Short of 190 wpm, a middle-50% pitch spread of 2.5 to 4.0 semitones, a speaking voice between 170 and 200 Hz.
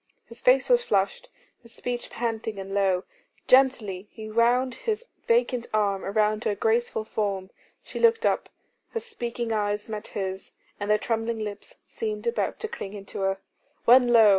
No: average, 165 wpm; average, 3.2 semitones; high, 225 Hz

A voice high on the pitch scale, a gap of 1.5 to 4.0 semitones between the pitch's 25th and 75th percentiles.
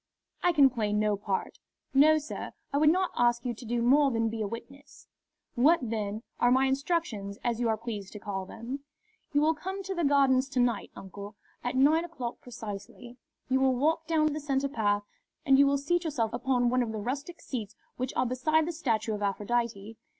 No: very high, 250 Hz; average, 4.5 semitones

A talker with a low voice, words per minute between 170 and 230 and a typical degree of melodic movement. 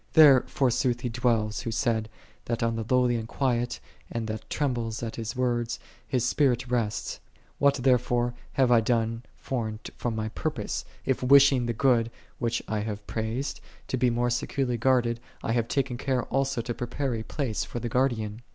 No: low, 120 Hz; average, 180 wpm; narrow, 2.0 semitones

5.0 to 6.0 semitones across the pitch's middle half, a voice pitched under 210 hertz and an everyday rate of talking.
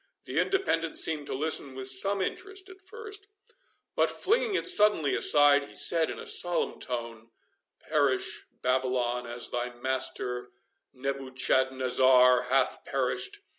No: wide, 5.6 semitones; low, 135 Hz; slow, 130 wpm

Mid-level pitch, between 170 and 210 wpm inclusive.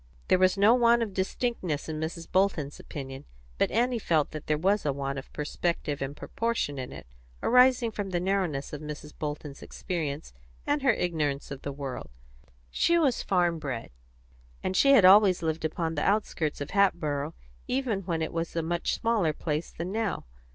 Yes: medium, 170 Hz; average, 180 wpm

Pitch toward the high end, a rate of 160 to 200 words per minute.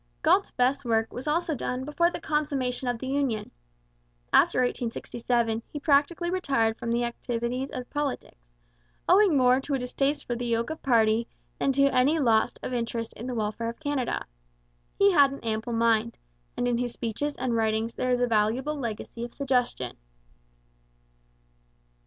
Yes: high, 245 Hz; average, 165 wpm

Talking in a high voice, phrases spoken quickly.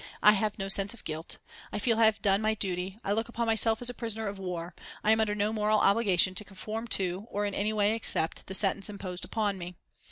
Yes: high, 205 Hz; fast, 245 wpm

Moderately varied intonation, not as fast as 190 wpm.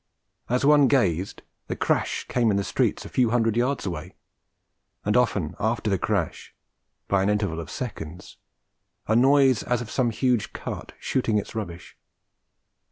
Yes: average, 4.3 semitones; average, 160 wpm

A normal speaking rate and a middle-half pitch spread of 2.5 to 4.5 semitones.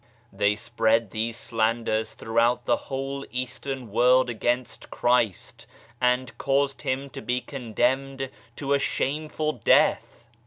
No: slow, 120 wpm; average, 2.9 semitones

